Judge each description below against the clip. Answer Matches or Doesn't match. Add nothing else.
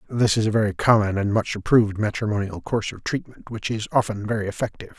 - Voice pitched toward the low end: Matches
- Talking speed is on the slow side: Doesn't match